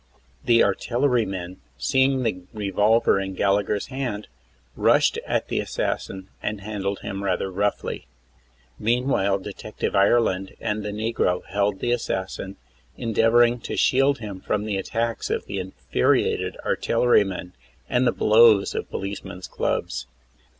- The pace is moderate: No, slow, 130 wpm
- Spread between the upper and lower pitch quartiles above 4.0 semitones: No, average, 3.2 semitones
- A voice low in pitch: Yes, low, 105 Hz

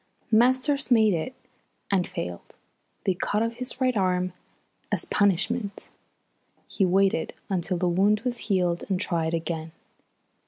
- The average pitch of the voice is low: No, high, 195 Hz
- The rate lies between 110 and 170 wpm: Yes, slow, 135 wpm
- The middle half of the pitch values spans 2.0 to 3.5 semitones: No, average, 4.7 semitones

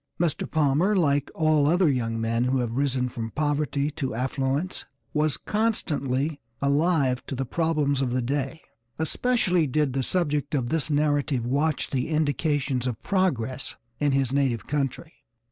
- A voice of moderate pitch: Yes, medium, 145 Hz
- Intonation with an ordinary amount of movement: Yes, average, 3.2 semitones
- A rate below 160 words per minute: Yes, average, 150 wpm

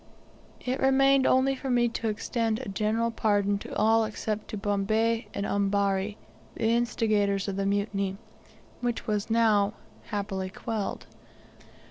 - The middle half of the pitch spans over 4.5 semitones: No, narrow, 2.4 semitones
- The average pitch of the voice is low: No, high, 215 Hz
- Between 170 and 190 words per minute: No, slow, 135 wpm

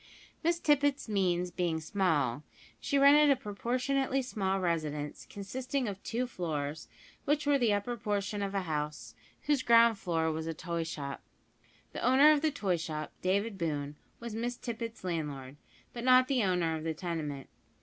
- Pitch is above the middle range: Yes, high, 195 Hz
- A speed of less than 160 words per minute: No, average, 165 wpm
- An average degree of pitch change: No, wide, 7.5 semitones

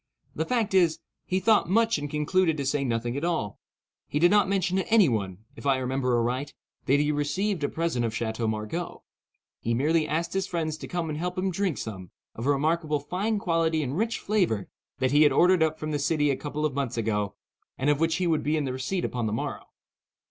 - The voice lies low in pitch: No, medium, 150 Hz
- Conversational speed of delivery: No, fast, 225 wpm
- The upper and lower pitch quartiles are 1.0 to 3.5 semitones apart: No, average, 5.2 semitones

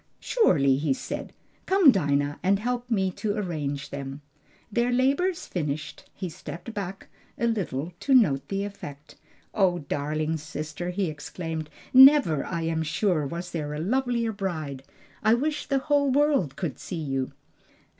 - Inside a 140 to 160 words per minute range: Yes, average, 150 wpm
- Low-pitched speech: No, medium, 175 Hz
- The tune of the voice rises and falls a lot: Yes, wide, 7.7 semitones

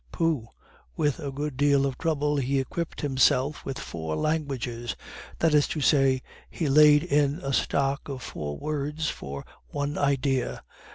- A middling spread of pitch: No, narrow, 2.1 semitones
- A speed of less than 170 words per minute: Yes, average, 155 wpm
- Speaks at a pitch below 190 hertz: Yes, medium, 140 Hz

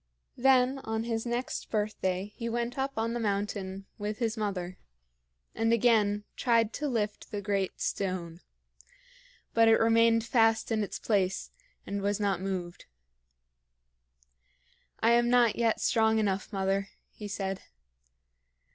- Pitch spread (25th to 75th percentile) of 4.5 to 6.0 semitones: No, average, 2.7 semitones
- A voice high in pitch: Yes, high, 215 Hz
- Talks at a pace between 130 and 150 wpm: Yes, slow, 135 wpm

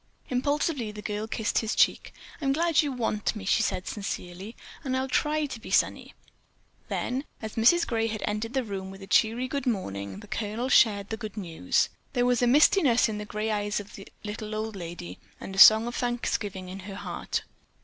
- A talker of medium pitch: No, high, 220 Hz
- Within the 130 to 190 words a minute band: No, average, 200 wpm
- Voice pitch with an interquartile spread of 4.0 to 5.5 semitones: No, average, 3.5 semitones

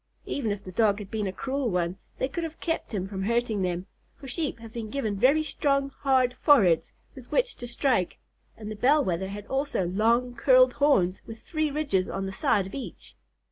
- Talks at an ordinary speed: No, fast, 210 wpm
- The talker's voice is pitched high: Yes, high, 235 Hz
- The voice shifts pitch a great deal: Yes, wide, 6.1 semitones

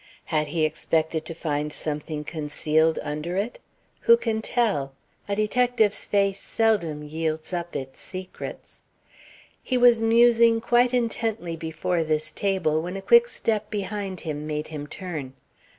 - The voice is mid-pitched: Yes, medium, 175 Hz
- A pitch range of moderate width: No, wide, 6.1 semitones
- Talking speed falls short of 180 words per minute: Yes, average, 140 wpm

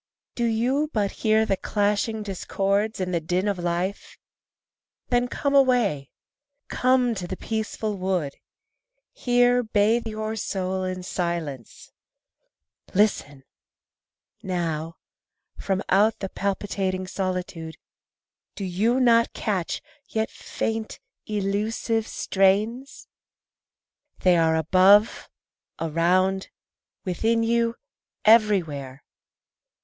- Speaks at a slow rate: Yes, slow, 95 wpm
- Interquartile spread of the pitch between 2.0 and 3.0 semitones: No, average, 3.5 semitones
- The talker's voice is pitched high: Yes, high, 200 Hz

